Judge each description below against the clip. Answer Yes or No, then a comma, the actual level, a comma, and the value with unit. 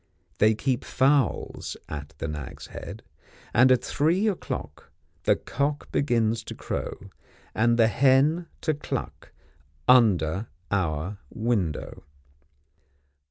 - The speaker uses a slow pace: Yes, slow, 110 wpm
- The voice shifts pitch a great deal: Yes, wide, 6.8 semitones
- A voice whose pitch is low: Yes, low, 115 Hz